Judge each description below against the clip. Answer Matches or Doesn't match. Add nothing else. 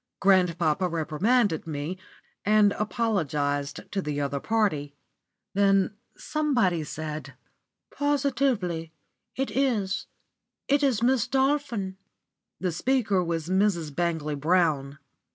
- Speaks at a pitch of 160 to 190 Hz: Matches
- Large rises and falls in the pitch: Matches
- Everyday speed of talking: Doesn't match